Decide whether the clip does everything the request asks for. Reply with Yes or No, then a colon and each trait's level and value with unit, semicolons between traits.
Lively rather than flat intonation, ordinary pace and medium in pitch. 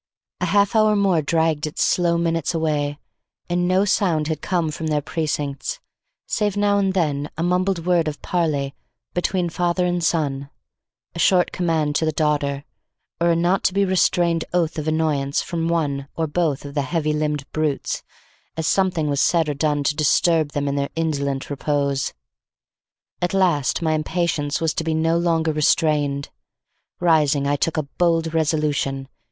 No: average, 2.9 semitones; average, 170 wpm; medium, 160 Hz